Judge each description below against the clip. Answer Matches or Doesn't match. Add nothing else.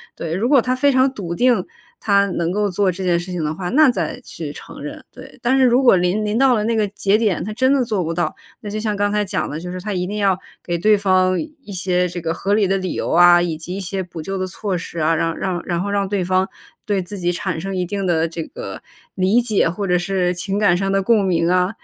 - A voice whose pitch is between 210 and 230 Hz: Doesn't match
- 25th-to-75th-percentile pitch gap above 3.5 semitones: Doesn't match